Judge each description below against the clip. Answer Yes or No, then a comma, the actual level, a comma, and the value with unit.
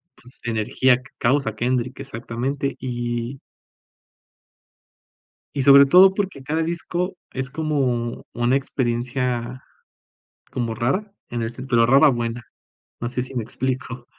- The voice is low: Yes, low, 125 Hz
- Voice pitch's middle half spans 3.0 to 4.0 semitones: No, narrow, 2.5 semitones